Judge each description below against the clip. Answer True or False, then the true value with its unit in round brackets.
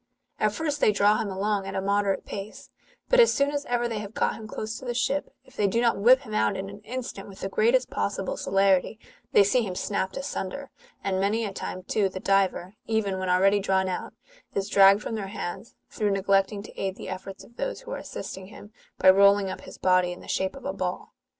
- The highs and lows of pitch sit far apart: False (2.8 semitones)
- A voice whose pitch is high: True (200 Hz)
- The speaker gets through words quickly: True (235 wpm)